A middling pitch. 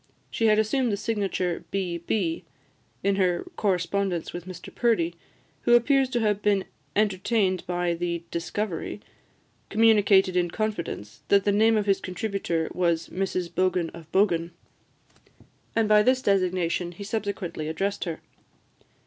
No: high, 195 Hz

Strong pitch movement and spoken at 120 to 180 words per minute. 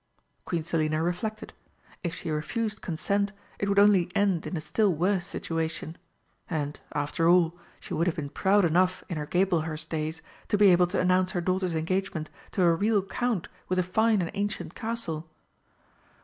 No: average, 3.6 semitones; average, 175 wpm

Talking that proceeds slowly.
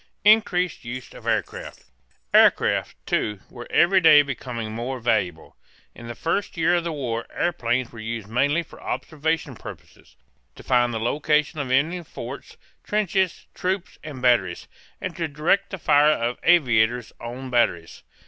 No: average, 155 wpm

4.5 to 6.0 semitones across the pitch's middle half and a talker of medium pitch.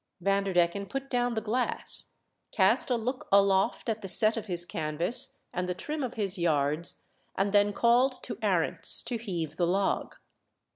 No: average, 5.0 semitones; high, 200 Hz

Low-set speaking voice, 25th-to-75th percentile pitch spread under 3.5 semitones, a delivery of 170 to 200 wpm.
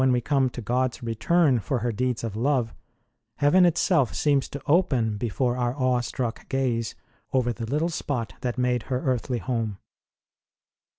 Yes: low, 125 Hz; narrow, 2.6 semitones; average, 180 wpm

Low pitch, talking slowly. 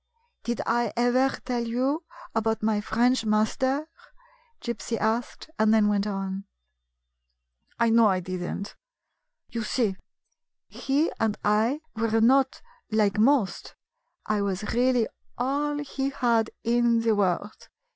No: high, 230 Hz; slow, 130 wpm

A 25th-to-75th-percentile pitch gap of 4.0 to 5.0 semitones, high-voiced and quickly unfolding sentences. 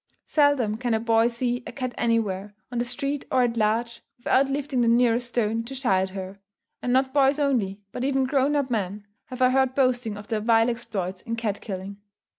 No: average, 3.4 semitones; high, 240 Hz; fast, 215 wpm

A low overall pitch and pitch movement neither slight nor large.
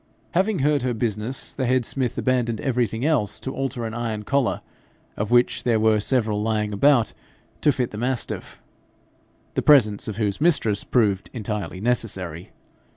Yes: low, 120 Hz; average, 3.6 semitones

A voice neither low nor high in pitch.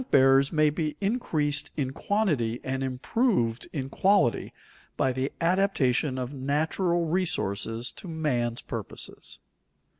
Yes: medium, 145 Hz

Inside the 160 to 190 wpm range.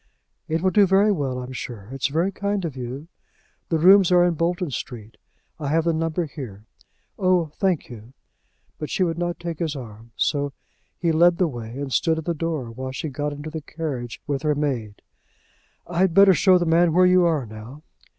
No: average, 200 wpm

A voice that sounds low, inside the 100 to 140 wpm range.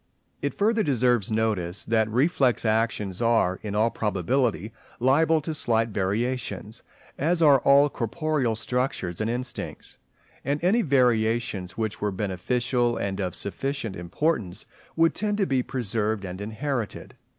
Yes: low, 115 Hz; slow, 135 wpm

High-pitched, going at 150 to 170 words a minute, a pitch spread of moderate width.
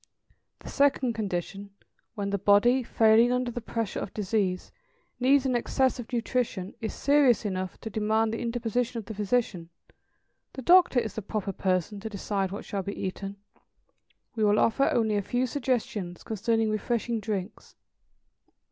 Yes: high, 220 Hz; average, 155 wpm; average, 3.3 semitones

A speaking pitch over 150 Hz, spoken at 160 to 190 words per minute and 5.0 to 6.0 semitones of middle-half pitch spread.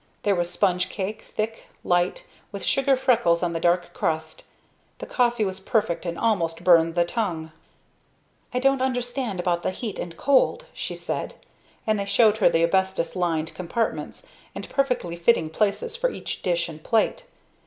Yes: high, 190 Hz; average, 165 wpm; wide, 5.5 semitones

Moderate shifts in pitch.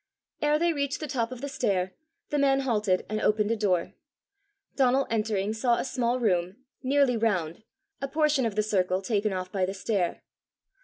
No: wide, 5.7 semitones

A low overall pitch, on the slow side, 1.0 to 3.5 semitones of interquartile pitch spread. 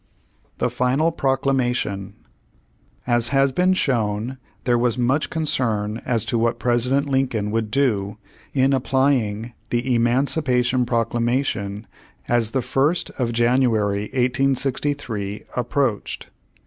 Yes: low, 125 Hz; slow, 110 wpm; average, 3.0 semitones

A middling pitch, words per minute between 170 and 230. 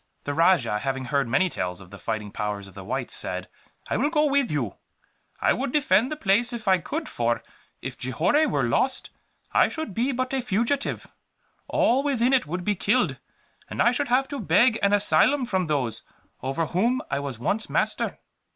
No: high, 195 Hz; average, 195 wpm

